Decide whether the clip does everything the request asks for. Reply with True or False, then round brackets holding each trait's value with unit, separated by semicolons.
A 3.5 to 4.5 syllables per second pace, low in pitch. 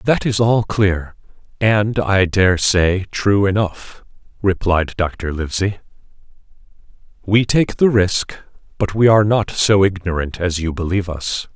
True (4.1 syllables/s; 95 Hz)